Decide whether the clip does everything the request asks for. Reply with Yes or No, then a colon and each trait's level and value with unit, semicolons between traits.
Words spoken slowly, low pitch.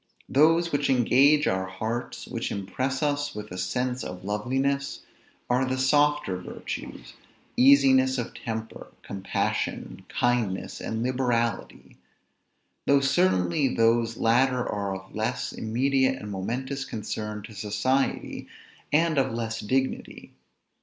Yes: slow, 120 wpm; low, 125 Hz